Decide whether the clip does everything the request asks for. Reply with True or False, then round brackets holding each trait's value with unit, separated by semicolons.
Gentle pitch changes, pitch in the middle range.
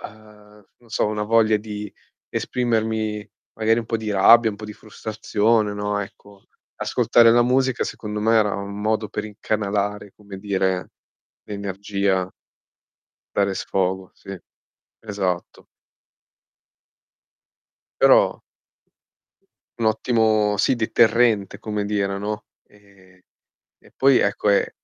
False (1.7 semitones; 105 Hz)